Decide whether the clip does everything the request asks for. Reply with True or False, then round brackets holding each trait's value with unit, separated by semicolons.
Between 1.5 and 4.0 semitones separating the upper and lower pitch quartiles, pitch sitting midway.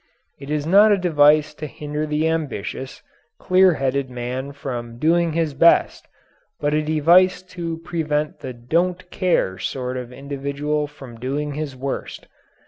True (3.6 semitones; 150 Hz)